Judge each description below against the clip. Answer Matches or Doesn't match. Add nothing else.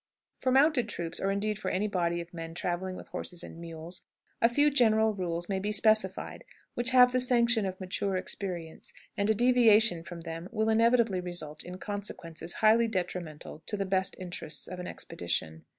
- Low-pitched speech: Doesn't match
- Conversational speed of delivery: Matches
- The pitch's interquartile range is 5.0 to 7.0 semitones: Doesn't match